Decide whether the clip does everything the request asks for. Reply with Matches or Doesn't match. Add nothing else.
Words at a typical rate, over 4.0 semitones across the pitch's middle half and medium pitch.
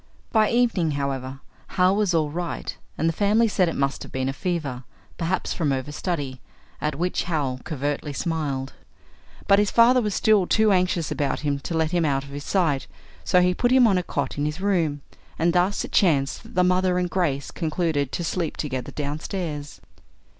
Matches